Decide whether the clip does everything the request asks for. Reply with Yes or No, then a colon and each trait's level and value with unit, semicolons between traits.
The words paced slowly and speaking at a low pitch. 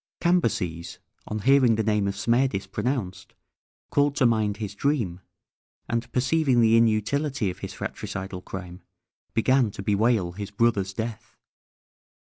Yes: slow, 130 wpm; low, 110 Hz